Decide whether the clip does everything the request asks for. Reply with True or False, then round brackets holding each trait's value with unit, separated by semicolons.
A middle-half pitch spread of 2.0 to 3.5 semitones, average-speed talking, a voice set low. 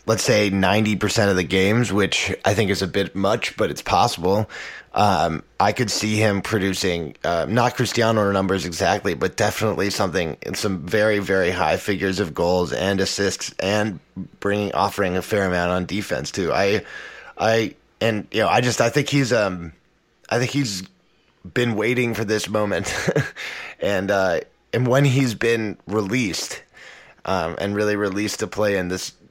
True (2.4 semitones; 170 wpm; 100 Hz)